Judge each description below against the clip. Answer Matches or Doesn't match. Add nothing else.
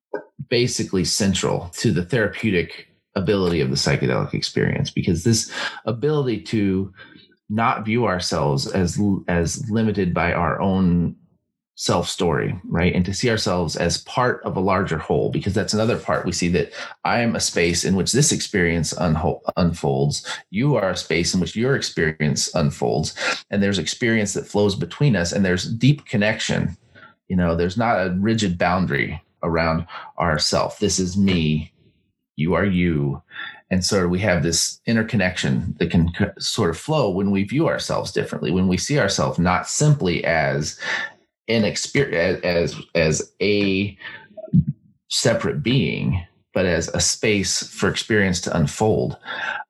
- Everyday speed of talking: Matches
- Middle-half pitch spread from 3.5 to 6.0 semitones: Matches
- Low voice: Matches